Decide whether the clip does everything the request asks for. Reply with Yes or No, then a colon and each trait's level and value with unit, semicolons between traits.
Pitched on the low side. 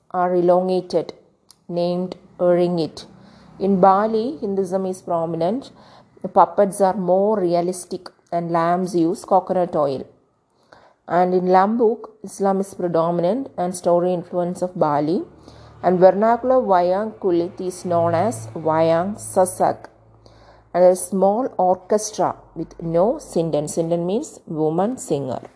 No: medium, 180 Hz